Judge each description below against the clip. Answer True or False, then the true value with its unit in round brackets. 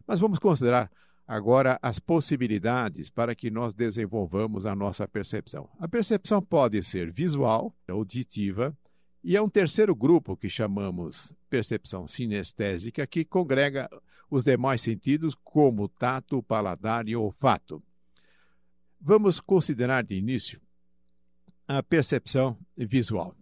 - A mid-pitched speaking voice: False (120 Hz)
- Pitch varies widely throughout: True (5.9 semitones)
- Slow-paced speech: True (115 wpm)